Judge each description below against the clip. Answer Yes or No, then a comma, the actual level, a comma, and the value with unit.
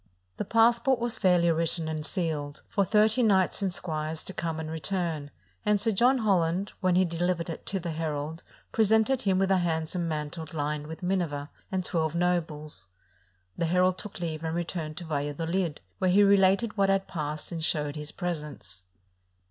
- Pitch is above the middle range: No, medium, 170 Hz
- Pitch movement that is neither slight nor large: Yes, average, 3.5 semitones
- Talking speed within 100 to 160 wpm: No, average, 180 wpm